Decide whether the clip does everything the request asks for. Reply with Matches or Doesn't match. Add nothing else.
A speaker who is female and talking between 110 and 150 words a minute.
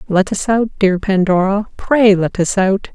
Doesn't match